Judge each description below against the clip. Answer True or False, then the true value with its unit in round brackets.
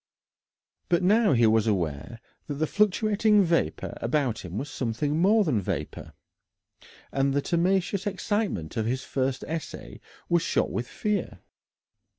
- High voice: False (145 Hz)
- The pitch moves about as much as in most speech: False (8.9 semitones)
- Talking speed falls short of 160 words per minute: True (140 wpm)